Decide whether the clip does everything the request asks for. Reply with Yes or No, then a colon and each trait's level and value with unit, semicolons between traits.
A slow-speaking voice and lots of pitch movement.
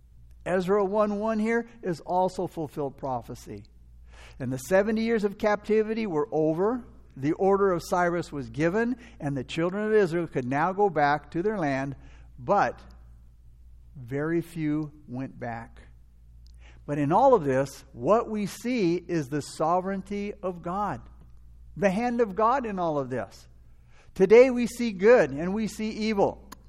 No: average, 150 wpm; wide, 8.8 semitones